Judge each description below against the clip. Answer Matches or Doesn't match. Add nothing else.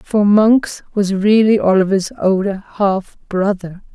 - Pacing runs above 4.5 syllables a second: Doesn't match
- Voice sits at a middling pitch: Doesn't match